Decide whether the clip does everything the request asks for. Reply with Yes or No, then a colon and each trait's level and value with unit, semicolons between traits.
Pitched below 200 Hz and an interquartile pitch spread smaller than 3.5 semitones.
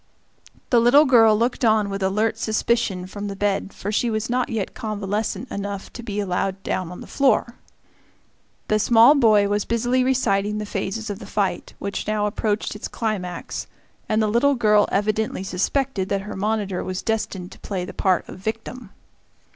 No: high, 210 Hz; narrow, 2.5 semitones